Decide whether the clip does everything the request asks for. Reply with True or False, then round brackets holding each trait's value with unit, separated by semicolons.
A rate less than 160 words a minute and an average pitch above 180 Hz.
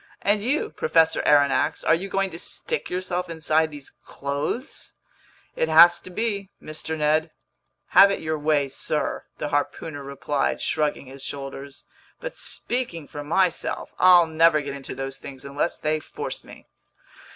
False (150 wpm; 155 Hz)